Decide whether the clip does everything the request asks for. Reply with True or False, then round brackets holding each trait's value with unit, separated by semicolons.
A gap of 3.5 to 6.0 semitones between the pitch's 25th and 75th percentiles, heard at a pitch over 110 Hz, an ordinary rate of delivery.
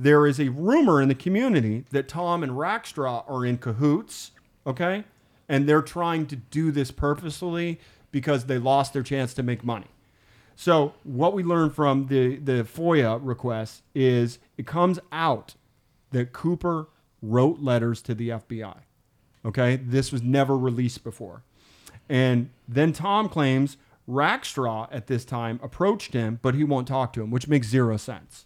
True (3.8 semitones; 135 Hz; 160 wpm)